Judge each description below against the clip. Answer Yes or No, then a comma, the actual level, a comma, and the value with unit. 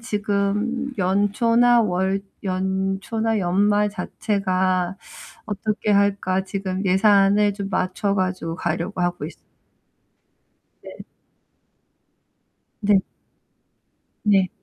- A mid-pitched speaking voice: No, high, 200 Hz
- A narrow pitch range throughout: Yes, narrow, 2.0 semitones